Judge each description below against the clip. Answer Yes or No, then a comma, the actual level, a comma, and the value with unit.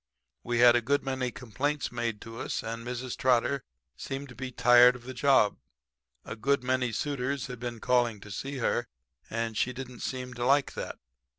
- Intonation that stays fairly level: Yes, narrow, 1.8 semitones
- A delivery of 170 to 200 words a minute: Yes, average, 190 wpm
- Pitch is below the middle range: Yes, low, 125 Hz